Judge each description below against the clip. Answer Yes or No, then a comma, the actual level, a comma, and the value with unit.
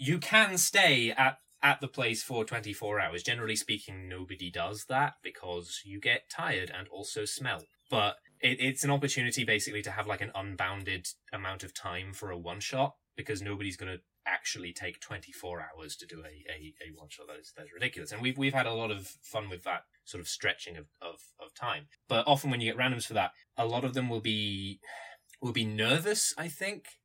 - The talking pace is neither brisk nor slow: No, fast, 210 wpm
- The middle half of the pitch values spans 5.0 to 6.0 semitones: Yes, average, 5.3 semitones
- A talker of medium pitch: No, low, 110 Hz